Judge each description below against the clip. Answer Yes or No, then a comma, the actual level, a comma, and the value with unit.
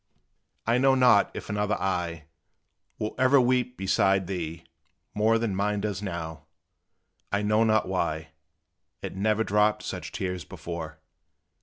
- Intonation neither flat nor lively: Yes, average, 3.7 semitones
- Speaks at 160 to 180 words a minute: No, slow, 135 wpm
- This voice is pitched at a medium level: No, low, 100 Hz